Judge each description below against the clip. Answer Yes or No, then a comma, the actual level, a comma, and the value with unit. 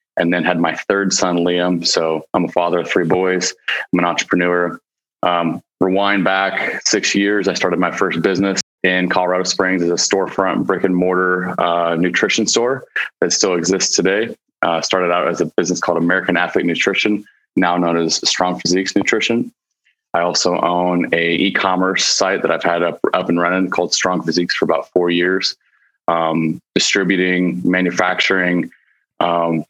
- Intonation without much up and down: Yes, narrow, 1.3 semitones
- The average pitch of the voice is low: Yes, very low, 90 Hz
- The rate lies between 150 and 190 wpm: Yes, average, 170 wpm